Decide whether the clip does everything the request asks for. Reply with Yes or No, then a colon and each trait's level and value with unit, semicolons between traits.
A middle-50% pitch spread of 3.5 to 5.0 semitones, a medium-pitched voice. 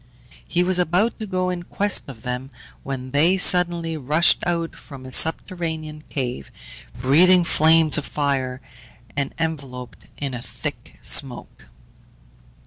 Yes: average, 4.6 semitones; medium, 155 Hz